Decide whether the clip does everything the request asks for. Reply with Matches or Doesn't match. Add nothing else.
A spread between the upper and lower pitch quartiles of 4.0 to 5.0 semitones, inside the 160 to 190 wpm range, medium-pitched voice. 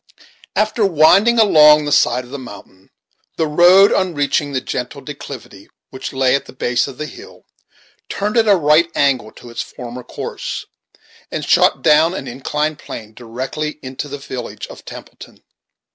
Matches